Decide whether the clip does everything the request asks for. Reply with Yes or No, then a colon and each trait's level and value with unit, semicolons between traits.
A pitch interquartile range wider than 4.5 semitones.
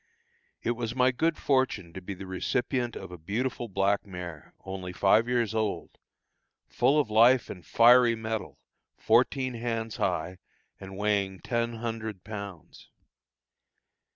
No: average, 3.9 semitones